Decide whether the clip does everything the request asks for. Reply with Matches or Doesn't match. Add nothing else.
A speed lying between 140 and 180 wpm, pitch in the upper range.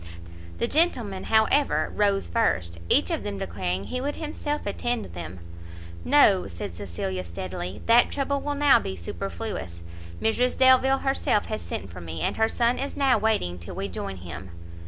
Matches